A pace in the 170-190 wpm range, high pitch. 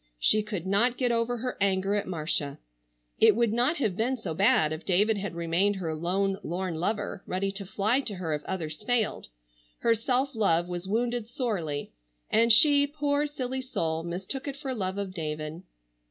Yes: average, 185 wpm; high, 200 Hz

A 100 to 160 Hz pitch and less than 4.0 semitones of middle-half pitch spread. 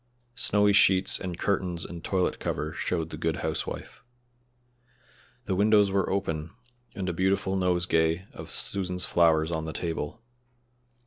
No: very low, 90 Hz; average, 2.8 semitones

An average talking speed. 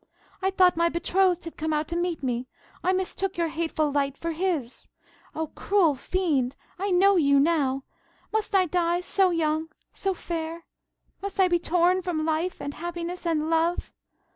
Yes: average, 170 wpm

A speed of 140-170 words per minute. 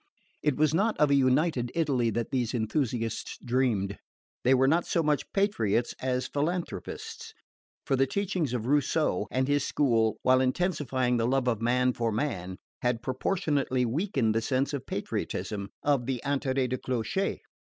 Yes: average, 160 wpm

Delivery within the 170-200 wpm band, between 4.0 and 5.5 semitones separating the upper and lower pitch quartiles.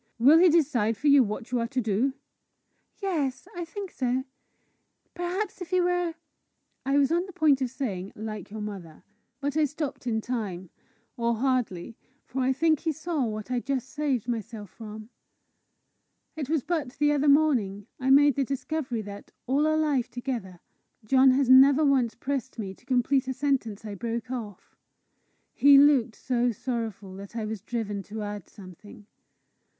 Yes: average, 175 wpm; average, 4.7 semitones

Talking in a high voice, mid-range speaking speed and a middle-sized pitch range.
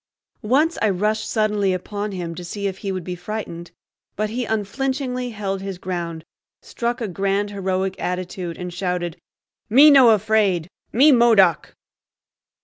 Yes: high, 200 Hz; average, 145 wpm; average, 3.5 semitones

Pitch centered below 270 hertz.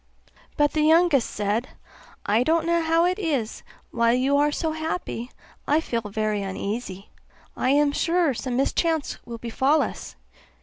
No: very high, 280 Hz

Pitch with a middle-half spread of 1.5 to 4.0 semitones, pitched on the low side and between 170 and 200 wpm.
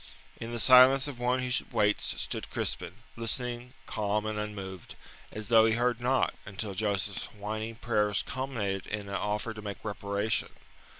No: average, 2.8 semitones; low, 110 Hz; average, 160 wpm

